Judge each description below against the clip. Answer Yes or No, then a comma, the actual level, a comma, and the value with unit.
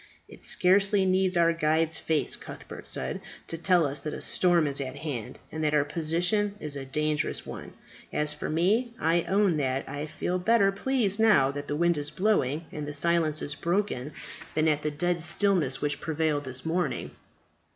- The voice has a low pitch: No, medium, 160 Hz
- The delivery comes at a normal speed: Yes, average, 185 wpm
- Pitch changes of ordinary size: Yes, average, 3.8 semitones